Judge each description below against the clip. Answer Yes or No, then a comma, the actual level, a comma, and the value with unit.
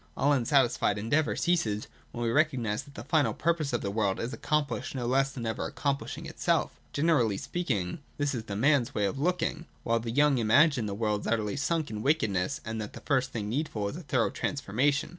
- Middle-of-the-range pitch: No, low, 125 Hz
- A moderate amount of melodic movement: Yes, average, 5.0 semitones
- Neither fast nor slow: No, fast, 215 wpm